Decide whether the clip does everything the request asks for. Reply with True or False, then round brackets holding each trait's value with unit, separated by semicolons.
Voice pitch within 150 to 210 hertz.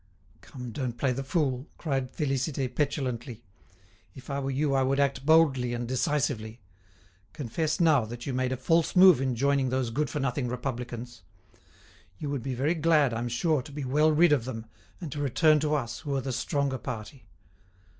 False (135 Hz)